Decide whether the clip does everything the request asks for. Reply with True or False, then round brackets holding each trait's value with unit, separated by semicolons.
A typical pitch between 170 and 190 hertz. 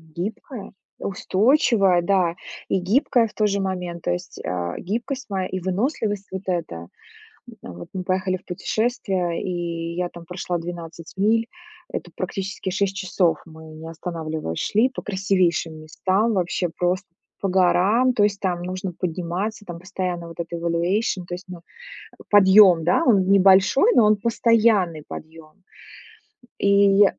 True (185 Hz)